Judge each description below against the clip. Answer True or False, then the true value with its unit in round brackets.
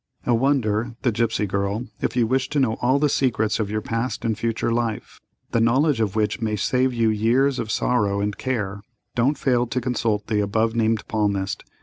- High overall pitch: False (115 Hz)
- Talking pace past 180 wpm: True (190 wpm)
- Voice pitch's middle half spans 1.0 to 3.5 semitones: True (2.8 semitones)